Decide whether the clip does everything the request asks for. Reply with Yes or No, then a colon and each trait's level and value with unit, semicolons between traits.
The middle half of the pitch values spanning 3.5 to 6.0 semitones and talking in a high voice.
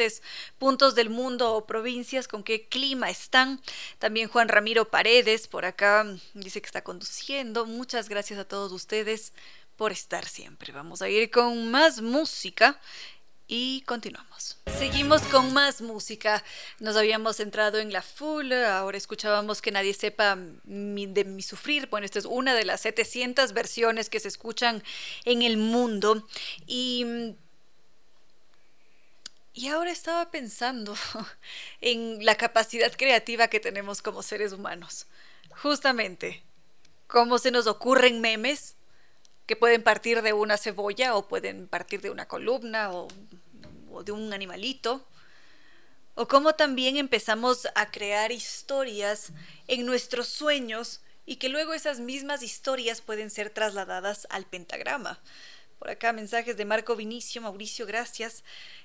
No: average, 3.0 semitones; high, 225 Hz